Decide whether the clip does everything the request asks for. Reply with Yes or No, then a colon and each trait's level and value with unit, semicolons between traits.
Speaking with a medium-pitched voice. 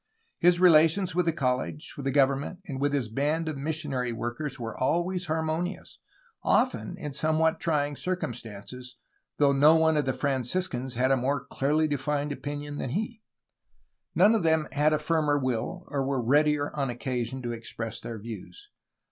Yes: medium, 145 Hz